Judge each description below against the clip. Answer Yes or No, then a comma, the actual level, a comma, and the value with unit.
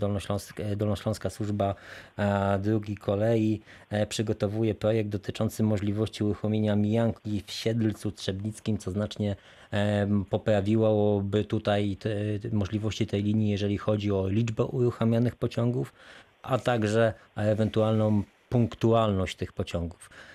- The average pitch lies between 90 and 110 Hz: Yes, low, 105 Hz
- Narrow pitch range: Yes, narrow, 1.3 semitones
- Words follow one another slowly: Yes, slow, 105 wpm